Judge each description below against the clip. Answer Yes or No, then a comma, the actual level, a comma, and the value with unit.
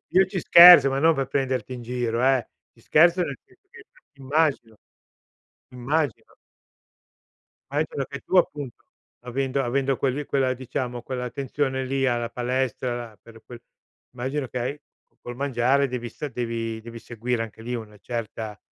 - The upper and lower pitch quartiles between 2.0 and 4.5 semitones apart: Yes, average, 2.7 semitones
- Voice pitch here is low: Yes, low, 130 Hz